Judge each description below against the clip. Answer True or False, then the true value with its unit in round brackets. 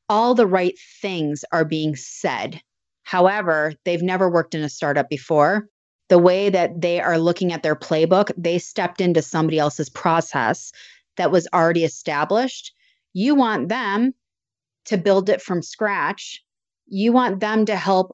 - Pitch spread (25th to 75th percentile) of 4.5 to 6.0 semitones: True (4.8 semitones)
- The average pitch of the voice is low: False (180 Hz)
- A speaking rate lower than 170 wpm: True (155 wpm)